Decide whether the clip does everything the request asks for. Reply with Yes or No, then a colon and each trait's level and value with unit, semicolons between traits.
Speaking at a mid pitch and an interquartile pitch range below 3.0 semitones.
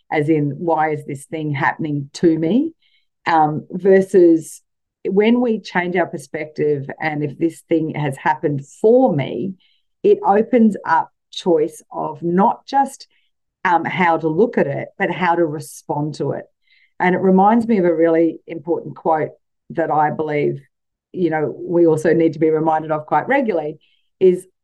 No: medium, 165 Hz; average, 3.7 semitones